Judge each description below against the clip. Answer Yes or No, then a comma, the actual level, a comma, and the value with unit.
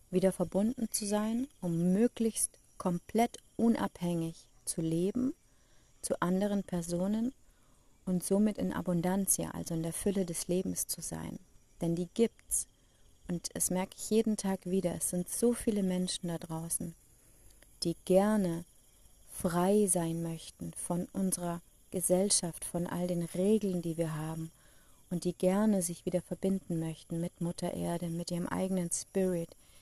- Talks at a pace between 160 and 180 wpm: No, average, 145 wpm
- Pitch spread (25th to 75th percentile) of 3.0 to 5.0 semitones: No, narrow, 2.4 semitones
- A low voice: No, medium, 180 Hz